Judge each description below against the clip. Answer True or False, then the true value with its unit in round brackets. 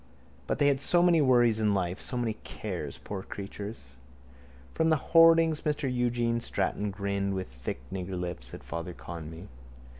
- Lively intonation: True (6.5 semitones)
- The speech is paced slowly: False (160 wpm)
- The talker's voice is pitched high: False (105 Hz)